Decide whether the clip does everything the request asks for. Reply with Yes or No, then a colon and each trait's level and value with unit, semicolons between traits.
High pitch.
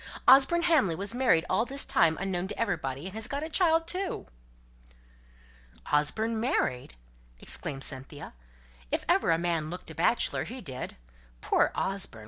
Yes: high, 195 Hz